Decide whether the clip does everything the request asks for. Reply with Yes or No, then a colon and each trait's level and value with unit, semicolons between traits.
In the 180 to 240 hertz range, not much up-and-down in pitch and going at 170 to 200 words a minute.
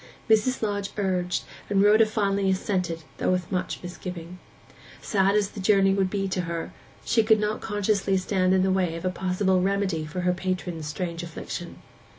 Yes: high, 190 Hz; narrow, 2.0 semitones; average, 175 wpm